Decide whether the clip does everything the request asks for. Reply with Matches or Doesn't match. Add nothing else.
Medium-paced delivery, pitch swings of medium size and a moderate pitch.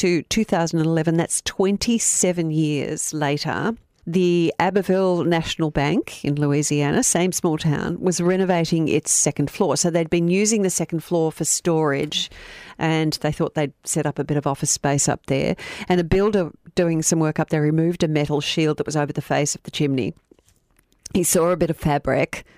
Matches